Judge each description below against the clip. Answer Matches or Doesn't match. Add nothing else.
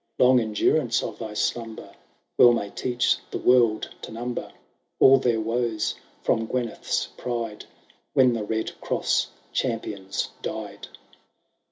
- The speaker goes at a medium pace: Doesn't match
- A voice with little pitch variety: Matches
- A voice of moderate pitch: Doesn't match